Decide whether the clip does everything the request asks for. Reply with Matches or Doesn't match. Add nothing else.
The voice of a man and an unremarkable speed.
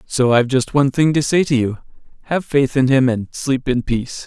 Doesn't match